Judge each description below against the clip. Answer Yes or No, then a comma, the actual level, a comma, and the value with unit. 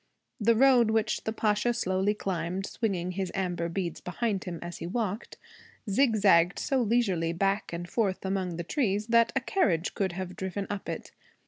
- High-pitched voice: Yes, high, 195 Hz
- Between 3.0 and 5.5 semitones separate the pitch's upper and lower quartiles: Yes, average, 3.8 semitones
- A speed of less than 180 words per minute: Yes, average, 170 wpm